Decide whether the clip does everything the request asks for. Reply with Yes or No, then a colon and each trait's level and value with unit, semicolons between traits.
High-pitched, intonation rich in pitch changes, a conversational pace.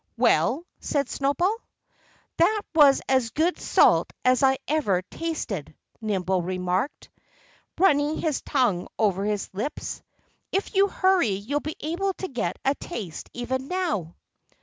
No: very high, 270 Hz; wide, 8.4 semitones; slow, 130 wpm